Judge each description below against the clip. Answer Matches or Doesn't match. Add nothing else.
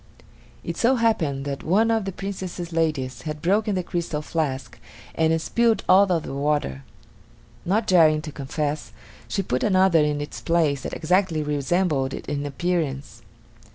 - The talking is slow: Doesn't match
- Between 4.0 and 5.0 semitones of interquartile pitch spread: Matches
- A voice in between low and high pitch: Matches